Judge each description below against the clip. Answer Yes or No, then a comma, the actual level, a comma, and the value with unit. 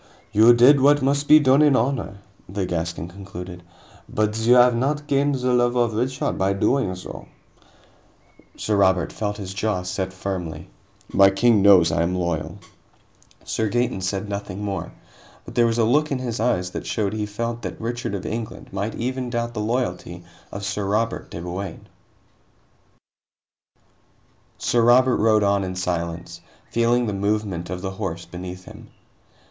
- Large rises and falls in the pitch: No, average, 4.3 semitones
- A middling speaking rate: Yes, average, 165 wpm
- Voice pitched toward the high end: No, low, 105 Hz